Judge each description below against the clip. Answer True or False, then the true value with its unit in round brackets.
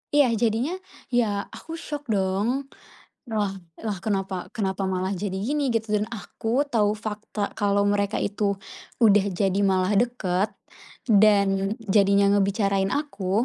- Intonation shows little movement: True (2.3 semitones)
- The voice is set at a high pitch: True (205 Hz)